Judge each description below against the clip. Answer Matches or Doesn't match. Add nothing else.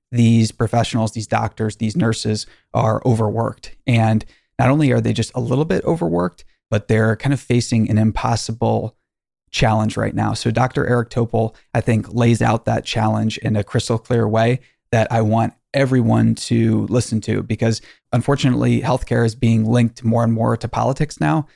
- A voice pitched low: Matches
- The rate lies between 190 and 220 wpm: Doesn't match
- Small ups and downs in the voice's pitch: Matches